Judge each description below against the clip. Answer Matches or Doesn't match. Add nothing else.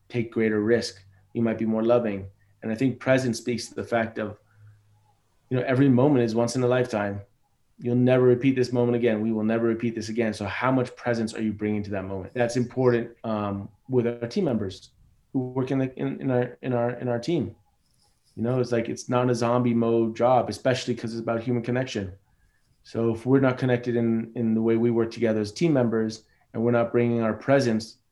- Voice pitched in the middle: Doesn't match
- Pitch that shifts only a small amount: Matches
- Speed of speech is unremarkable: Doesn't match